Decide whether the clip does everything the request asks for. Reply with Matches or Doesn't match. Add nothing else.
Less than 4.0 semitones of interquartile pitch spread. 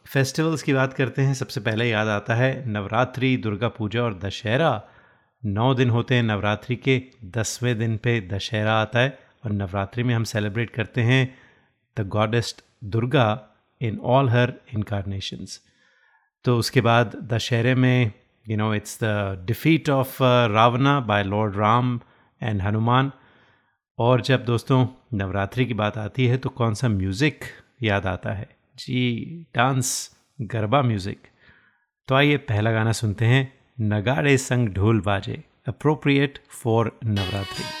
Matches